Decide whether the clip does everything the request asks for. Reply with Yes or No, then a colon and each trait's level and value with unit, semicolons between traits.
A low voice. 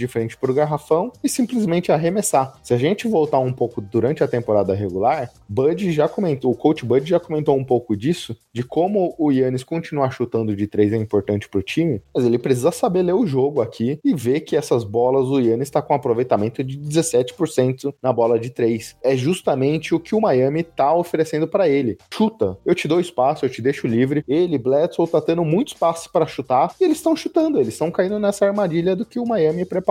No: medium, 150 Hz